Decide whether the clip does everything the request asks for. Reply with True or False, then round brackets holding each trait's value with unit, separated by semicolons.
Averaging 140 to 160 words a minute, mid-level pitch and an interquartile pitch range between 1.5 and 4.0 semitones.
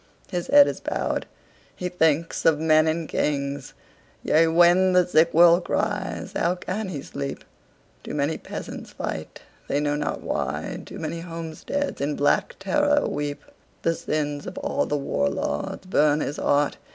True (145 wpm; 160 Hz; 3.7 semitones)